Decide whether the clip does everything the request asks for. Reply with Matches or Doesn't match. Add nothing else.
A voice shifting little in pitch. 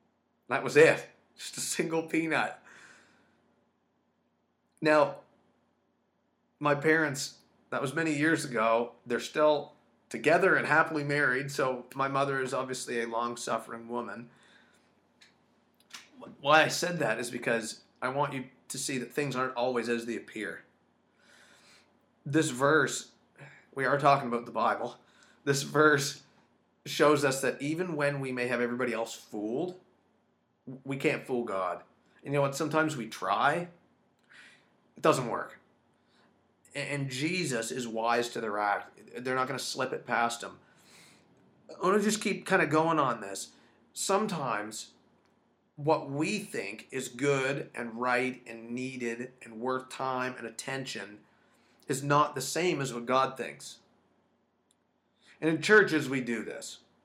Doesn't match